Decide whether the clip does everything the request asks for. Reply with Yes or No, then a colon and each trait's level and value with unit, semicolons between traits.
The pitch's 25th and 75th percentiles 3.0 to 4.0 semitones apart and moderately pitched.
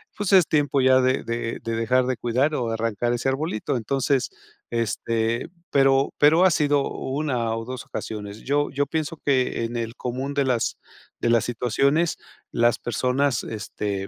No: average, 3.4 semitones; low, 125 Hz